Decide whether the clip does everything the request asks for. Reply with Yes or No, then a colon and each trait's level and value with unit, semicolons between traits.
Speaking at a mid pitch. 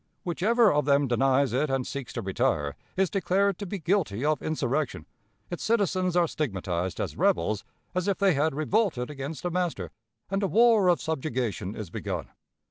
Yes: medium, 155 Hz